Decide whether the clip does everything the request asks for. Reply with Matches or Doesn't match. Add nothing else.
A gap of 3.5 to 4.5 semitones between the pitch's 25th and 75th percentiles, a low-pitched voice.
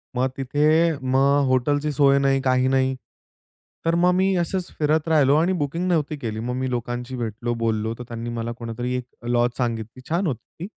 Matches